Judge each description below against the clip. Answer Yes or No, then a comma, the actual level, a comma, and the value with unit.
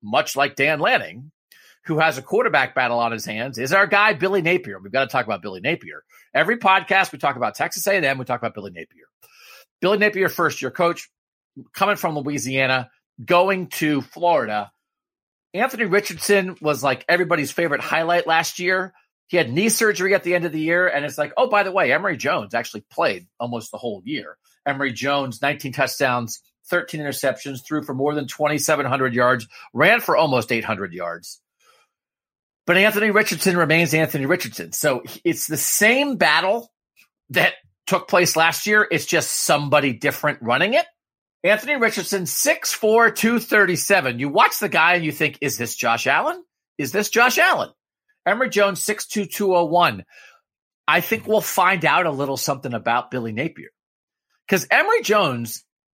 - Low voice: No, medium, 165 Hz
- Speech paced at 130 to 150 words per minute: No, average, 170 wpm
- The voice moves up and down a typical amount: No, wide, 6.7 semitones